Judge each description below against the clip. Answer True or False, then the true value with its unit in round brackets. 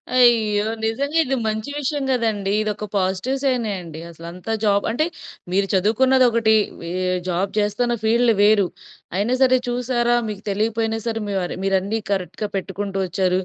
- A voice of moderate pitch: False (215 Hz)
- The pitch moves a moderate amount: True (3.5 semitones)